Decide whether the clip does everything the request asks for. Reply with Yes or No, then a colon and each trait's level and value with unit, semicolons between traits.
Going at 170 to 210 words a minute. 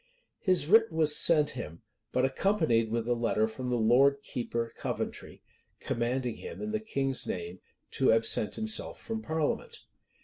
No: average, 150 wpm